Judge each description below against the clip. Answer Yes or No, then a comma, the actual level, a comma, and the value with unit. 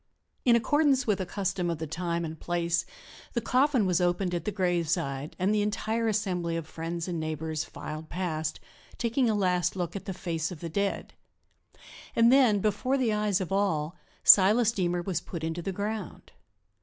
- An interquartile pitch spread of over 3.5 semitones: Yes, average, 4.0 semitones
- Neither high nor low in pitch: Yes, medium, 180 Hz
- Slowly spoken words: No, average, 180 wpm